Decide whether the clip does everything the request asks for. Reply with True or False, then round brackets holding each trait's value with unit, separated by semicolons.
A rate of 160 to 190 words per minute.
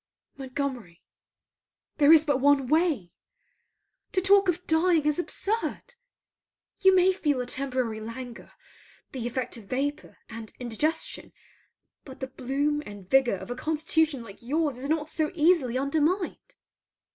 False (135 wpm)